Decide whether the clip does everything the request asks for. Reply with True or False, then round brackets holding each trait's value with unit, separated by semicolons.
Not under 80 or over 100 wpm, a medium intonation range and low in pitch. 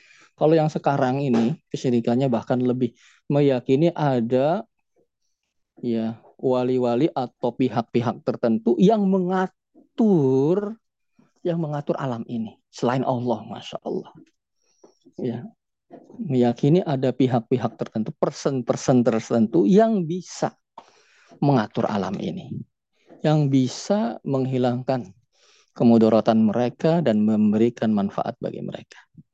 True (95 wpm; 4.4 semitones; 130 Hz)